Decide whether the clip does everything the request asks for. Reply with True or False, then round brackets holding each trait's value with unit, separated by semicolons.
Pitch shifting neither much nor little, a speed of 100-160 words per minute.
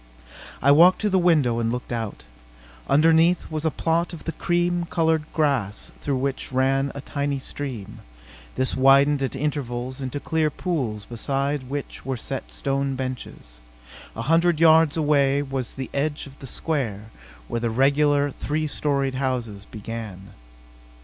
True (3.3 semitones; 150 wpm)